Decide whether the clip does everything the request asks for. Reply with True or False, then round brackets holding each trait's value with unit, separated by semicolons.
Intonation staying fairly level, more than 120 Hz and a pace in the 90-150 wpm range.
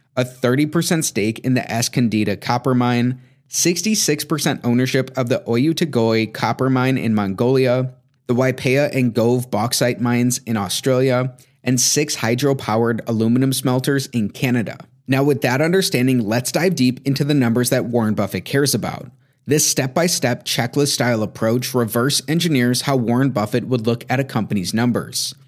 True (2.3 semitones; 130 Hz; 145 wpm)